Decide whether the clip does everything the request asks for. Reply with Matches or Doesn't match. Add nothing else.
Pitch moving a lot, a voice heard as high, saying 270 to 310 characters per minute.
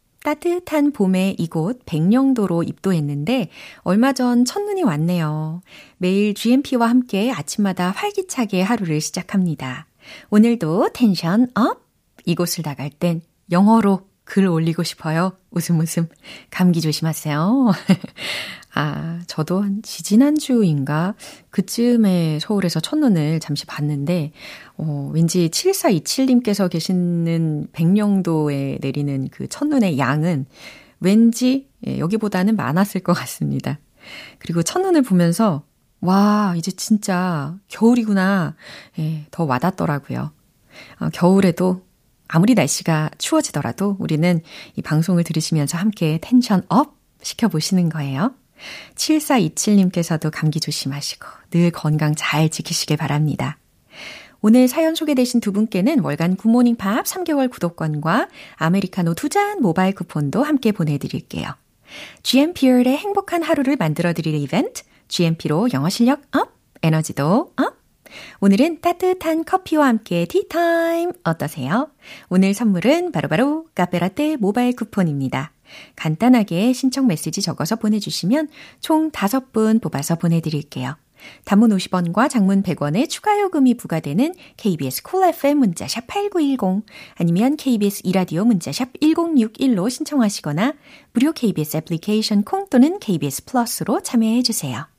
Matches